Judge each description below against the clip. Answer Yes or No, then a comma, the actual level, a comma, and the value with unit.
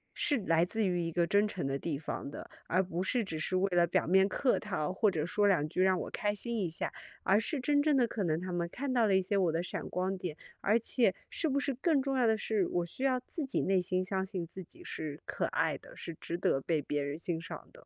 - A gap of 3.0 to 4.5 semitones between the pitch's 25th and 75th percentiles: No, average, 5.1 semitones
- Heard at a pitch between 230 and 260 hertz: No, high, 190 Hz